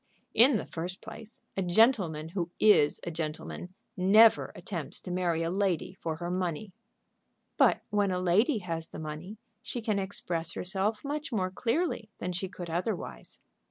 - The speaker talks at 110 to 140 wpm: No, average, 160 wpm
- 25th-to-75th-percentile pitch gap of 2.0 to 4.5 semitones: Yes, average, 3.9 semitones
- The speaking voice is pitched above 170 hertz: Yes, medium, 185 Hz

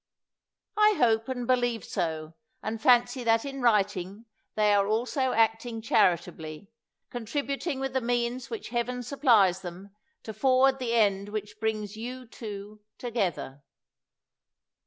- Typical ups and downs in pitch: Yes, average, 3.5 semitones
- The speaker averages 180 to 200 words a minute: No, slow, 135 wpm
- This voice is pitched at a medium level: No, high, 225 Hz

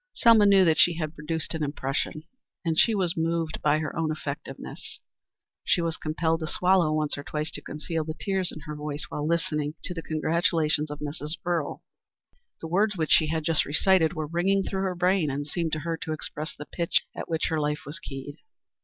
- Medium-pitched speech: Yes, medium, 160 Hz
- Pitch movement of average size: No, narrow, 2.2 semitones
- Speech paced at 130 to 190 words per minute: No, fast, 205 wpm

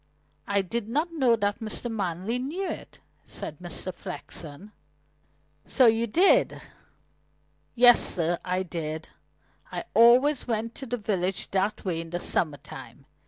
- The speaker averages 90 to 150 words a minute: Yes, average, 140 wpm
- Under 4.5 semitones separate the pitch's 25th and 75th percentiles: No, wide, 5.6 semitones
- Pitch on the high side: Yes, high, 215 Hz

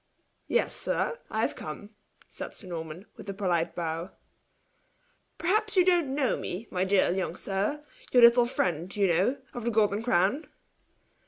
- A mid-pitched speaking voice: No, high, 205 Hz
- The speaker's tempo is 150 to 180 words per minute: Yes, average, 160 wpm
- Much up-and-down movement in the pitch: Yes, wide, 5.8 semitones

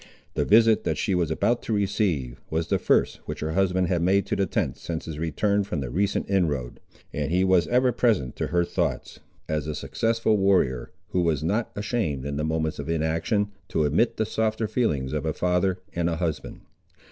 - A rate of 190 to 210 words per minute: Yes, fast, 205 wpm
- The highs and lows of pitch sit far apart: No, average, 4.8 semitones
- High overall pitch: No, very low, 85 Hz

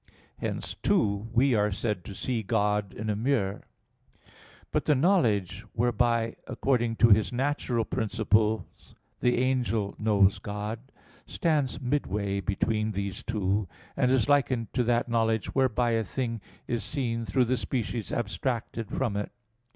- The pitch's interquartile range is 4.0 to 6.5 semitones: No, average, 3.2 semitones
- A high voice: No, low, 115 Hz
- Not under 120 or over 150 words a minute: Yes, average, 140 wpm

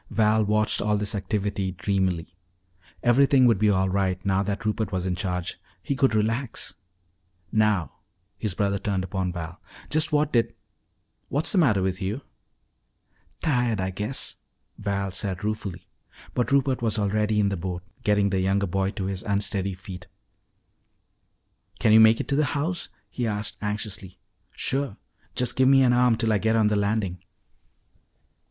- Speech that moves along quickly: No, average, 160 wpm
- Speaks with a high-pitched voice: No, low, 105 Hz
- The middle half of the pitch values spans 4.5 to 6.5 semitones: No, average, 3.1 semitones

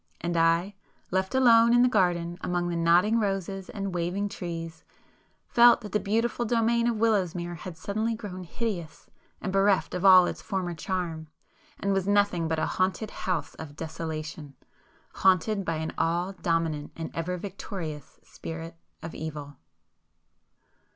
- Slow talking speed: No, average, 145 wpm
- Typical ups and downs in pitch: Yes, average, 3.5 semitones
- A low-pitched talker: No, medium, 180 Hz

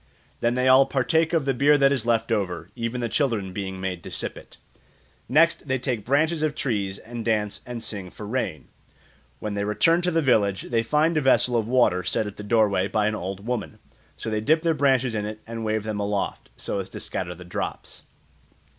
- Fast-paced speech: Yes, fast, 215 wpm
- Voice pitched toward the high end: No, low, 115 Hz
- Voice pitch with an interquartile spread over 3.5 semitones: Yes, average, 4.6 semitones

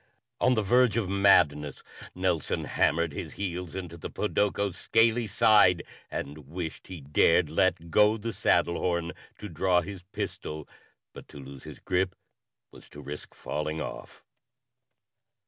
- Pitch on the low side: Yes, very low, 90 Hz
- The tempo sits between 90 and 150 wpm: Yes, average, 145 wpm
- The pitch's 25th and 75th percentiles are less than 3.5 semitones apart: No, average, 4.4 semitones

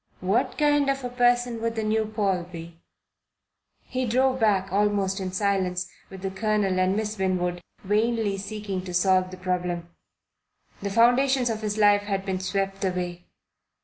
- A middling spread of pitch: Yes, average, 3.2 semitones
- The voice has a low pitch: No, high, 200 Hz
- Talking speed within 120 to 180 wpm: Yes, average, 160 wpm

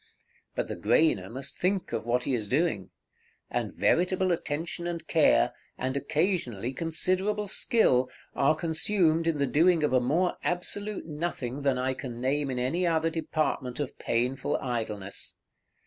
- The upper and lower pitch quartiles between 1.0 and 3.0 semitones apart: No, average, 5.3 semitones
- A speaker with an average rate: Yes, average, 150 wpm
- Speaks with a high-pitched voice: No, medium, 150 Hz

